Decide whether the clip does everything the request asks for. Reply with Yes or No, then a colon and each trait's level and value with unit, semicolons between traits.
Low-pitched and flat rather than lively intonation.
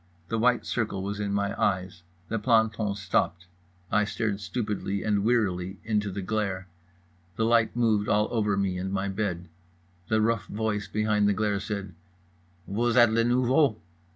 Yes: low, 105 Hz; narrow, 2.1 semitones